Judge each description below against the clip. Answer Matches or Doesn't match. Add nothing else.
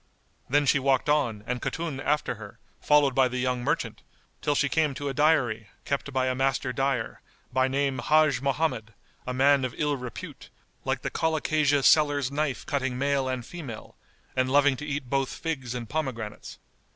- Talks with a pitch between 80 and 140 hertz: Matches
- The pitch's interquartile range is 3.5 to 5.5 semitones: Doesn't match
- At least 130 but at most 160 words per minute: Doesn't match